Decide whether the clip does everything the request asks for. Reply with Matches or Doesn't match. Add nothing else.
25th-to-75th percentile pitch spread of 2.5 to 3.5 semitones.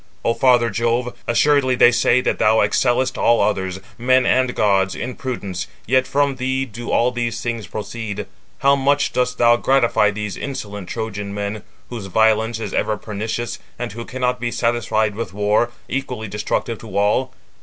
Matches